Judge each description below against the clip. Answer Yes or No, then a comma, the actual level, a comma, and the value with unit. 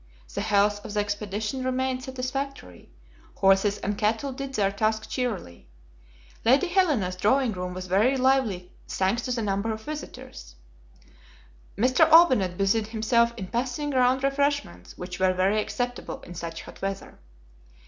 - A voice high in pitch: Yes, high, 220 Hz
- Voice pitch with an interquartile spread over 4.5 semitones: Yes, average, 5.0 semitones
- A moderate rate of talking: Yes, average, 145 wpm